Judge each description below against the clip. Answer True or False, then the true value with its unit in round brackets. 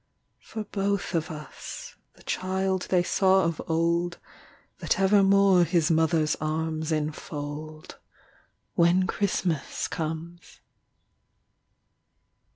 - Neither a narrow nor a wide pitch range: True (3.2 semitones)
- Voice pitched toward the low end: False (170 Hz)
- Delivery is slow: True (90 wpm)